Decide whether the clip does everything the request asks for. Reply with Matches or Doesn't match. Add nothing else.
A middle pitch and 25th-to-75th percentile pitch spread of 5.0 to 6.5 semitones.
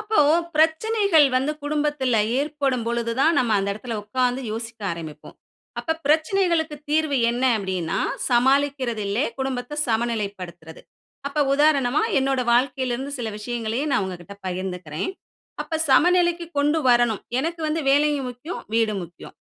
Doesn't match